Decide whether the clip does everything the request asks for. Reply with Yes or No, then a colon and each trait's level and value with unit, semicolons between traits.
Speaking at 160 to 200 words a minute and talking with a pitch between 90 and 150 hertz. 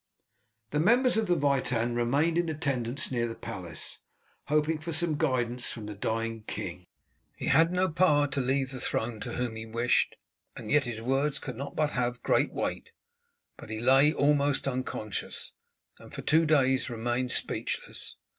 Yes: average, 170 wpm; low, 135 Hz